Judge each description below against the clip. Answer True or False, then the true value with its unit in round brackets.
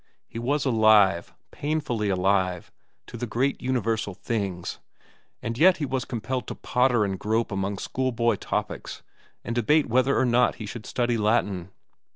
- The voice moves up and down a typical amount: True (3.8 semitones)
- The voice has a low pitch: True (115 Hz)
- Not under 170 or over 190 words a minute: False (155 wpm)